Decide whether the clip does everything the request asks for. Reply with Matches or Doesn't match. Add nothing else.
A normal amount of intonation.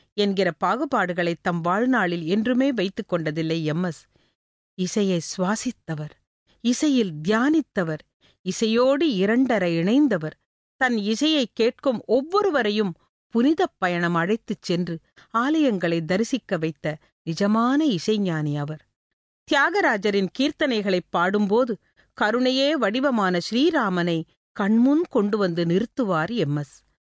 Doesn't match